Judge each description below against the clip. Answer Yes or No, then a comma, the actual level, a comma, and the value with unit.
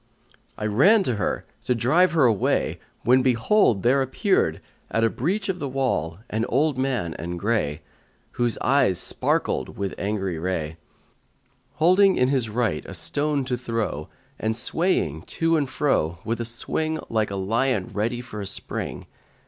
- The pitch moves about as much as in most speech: No, wide, 5.7 semitones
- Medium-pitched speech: No, low, 120 Hz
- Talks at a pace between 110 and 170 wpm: Yes, average, 160 wpm